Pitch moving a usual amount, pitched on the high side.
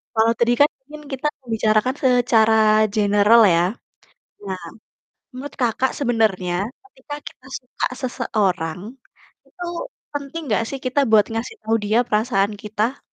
Yes: average, 3.6 semitones; high, 230 Hz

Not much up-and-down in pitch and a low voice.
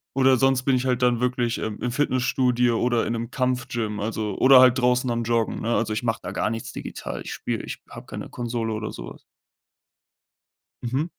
Yes: narrow, 2.0 semitones; low, 120 Hz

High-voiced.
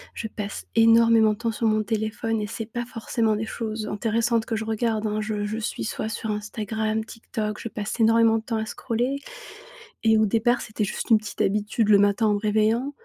Yes: high, 220 Hz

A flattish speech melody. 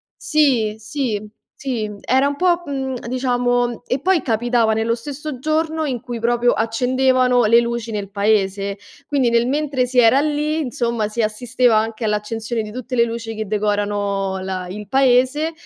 No: average, 3.5 semitones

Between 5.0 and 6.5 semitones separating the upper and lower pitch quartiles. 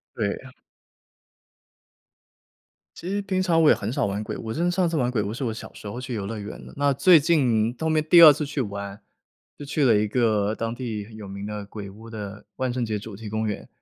Yes: wide, 5.6 semitones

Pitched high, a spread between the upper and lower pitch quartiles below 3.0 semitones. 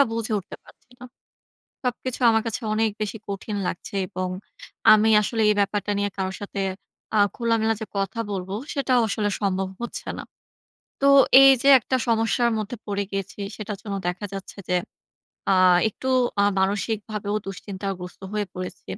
Yes: high, 210 Hz; narrow, 2.4 semitones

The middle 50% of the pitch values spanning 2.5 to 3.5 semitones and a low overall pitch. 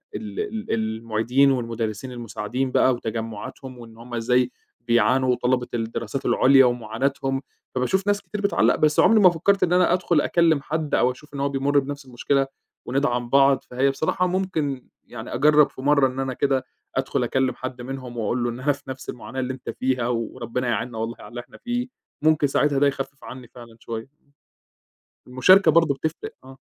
Yes: average, 3.0 semitones; low, 130 Hz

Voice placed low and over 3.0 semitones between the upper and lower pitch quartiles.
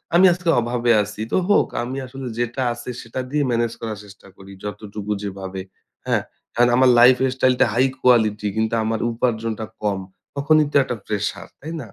Yes: low, 120 Hz; average, 3.5 semitones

